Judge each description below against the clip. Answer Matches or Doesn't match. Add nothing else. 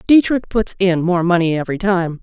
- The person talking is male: Doesn't match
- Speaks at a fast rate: Doesn't match